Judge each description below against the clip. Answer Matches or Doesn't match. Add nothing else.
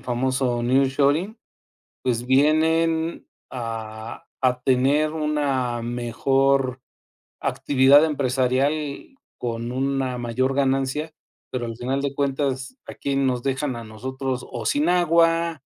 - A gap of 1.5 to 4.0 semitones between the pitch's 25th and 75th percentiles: Matches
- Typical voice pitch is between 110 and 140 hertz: Matches